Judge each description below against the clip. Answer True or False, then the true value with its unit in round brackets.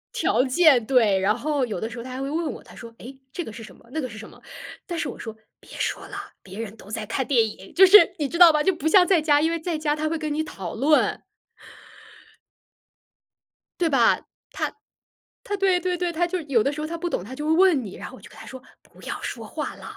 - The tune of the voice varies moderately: False (6.2 semitones)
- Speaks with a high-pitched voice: True (295 Hz)